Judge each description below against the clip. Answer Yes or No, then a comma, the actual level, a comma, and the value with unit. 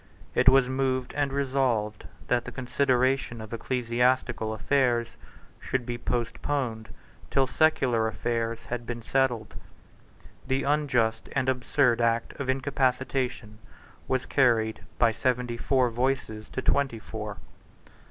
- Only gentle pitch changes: Yes, narrow, 2.3 semitones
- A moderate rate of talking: No, slow, 120 wpm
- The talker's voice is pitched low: Yes, low, 125 Hz